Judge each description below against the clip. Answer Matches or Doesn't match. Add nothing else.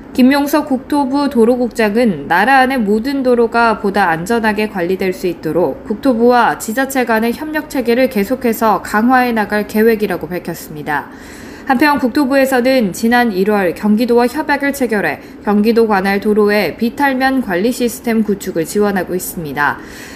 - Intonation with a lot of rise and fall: Doesn't match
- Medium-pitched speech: Doesn't match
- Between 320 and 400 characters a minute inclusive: Matches